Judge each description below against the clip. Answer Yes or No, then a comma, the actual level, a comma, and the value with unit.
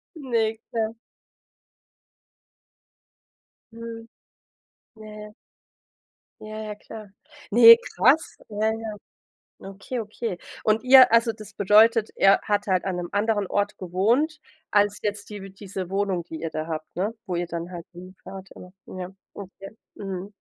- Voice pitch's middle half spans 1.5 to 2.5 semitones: No, average, 2.9 semitones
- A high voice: Yes, high, 205 Hz